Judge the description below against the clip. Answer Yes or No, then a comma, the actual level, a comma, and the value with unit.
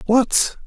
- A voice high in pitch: Yes, high, 240 Hz